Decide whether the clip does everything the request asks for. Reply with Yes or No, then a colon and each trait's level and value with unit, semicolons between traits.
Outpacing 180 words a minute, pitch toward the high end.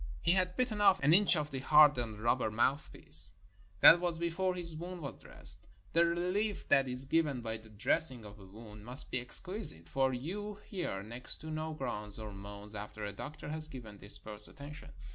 No: average, 195 wpm; low, 135 Hz